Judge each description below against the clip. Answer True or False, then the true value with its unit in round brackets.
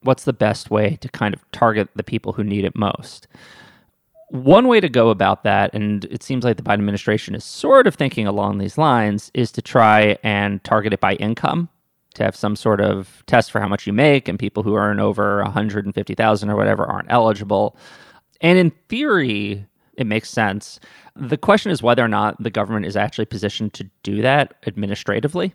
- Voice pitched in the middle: False (105 Hz)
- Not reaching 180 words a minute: False (195 wpm)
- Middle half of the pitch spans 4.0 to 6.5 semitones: False (2.8 semitones)